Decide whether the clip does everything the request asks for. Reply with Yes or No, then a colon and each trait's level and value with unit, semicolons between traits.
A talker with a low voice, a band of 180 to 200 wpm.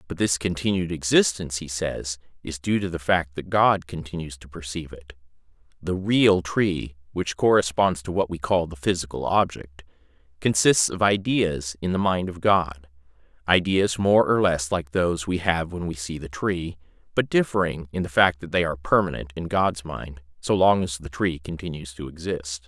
Yes: very low, 85 Hz; average, 185 wpm